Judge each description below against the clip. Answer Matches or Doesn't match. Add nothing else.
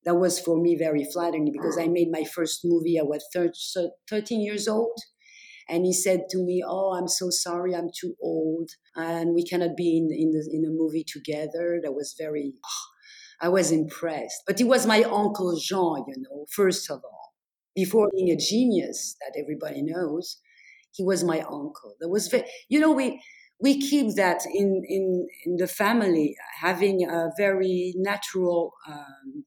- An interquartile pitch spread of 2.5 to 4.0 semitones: Matches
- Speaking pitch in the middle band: Matches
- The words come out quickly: Doesn't match